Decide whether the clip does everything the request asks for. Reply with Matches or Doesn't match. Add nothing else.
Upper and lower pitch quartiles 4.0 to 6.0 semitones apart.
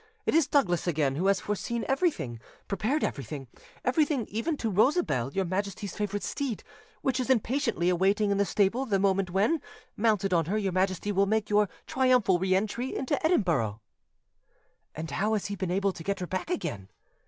Matches